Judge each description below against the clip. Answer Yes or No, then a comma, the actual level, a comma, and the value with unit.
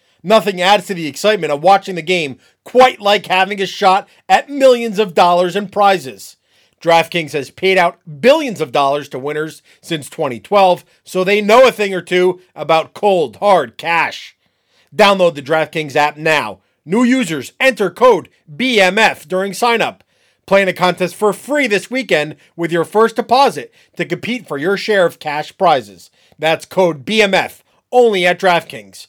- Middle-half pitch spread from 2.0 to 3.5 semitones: No, average, 4.4 semitones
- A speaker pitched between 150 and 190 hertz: Yes, medium, 185 Hz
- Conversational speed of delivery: Yes, average, 165 wpm